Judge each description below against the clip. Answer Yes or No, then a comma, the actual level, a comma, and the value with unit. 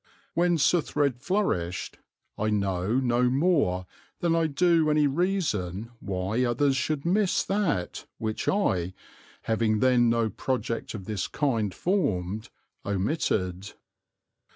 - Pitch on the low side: Yes, low, 120 Hz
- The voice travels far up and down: Yes, wide, 8.0 semitones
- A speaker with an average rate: No, slow, 115 wpm